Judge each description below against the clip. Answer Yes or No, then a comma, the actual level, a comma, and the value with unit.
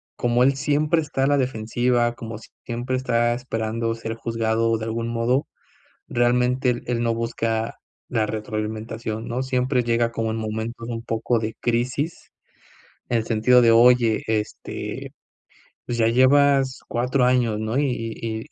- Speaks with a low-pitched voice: Yes, low, 120 Hz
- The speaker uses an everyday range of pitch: No, narrow, 1.9 semitones